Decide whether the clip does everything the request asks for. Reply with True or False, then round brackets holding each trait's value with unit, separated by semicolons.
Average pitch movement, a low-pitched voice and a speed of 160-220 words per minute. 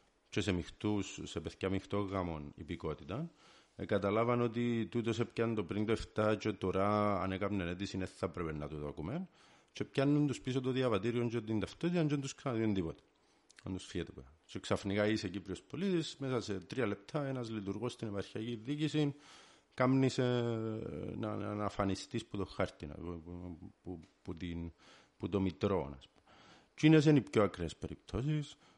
True (4.4 semitones; 105 Hz; 165 wpm)